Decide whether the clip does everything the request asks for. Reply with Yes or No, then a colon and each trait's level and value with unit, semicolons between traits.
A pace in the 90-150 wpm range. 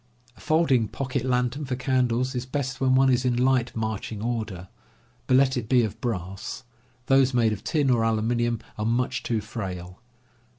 No: average, 175 wpm